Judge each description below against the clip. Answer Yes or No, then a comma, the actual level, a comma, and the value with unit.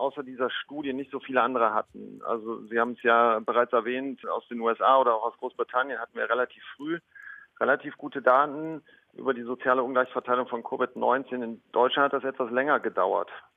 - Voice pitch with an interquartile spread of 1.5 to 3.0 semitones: Yes, narrow, 2.5 semitones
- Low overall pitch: Yes, low, 130 Hz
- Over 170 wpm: Yes, average, 185 wpm